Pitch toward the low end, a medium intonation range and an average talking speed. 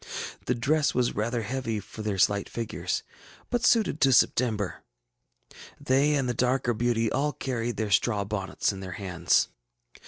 Yes: low, 120 Hz; average, 4.0 semitones; average, 155 wpm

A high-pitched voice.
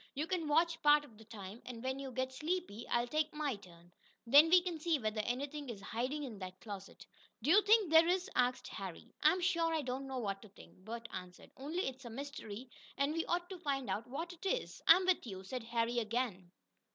Yes: very high, 265 Hz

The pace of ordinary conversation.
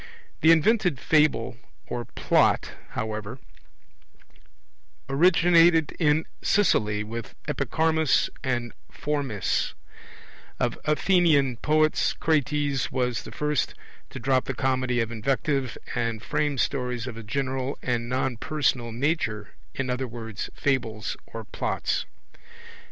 No: slow, 110 wpm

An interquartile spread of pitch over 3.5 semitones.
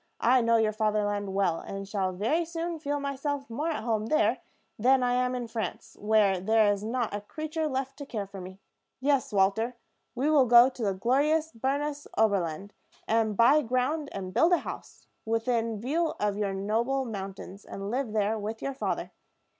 Yes: average, 4.9 semitones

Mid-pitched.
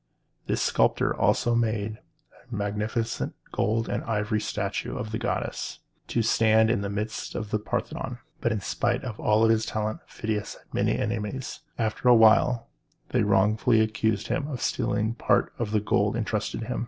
No: low, 110 Hz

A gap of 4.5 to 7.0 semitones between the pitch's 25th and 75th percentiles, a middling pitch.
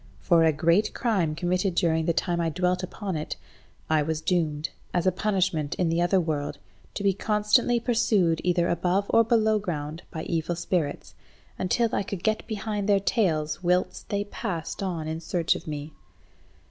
No: average, 3.8 semitones; medium, 175 Hz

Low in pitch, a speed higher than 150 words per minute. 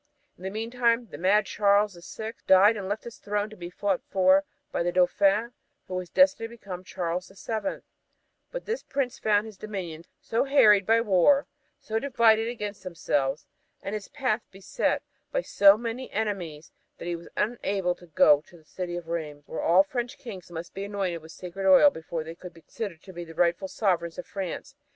No: high, 195 Hz; average, 195 wpm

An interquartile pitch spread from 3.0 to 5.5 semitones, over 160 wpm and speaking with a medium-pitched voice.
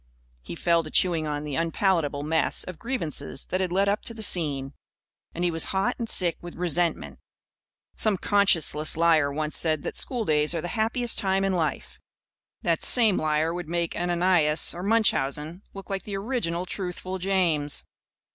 Yes: average, 3.9 semitones; average, 170 wpm; medium, 175 Hz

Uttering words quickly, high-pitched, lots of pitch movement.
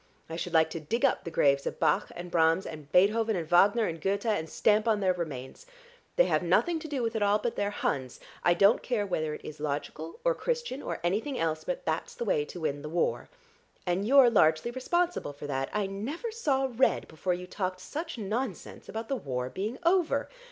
Yes: fast, 215 wpm; high, 200 Hz; wide, 7.5 semitones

